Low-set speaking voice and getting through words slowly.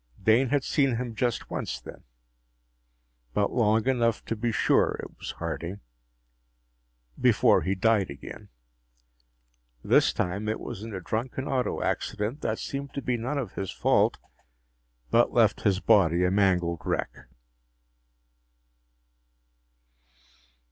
Yes: low, 110 Hz; slow, 125 wpm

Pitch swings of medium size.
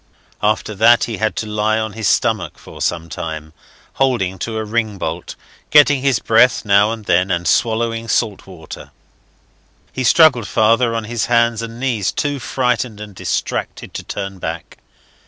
Yes: average, 3.0 semitones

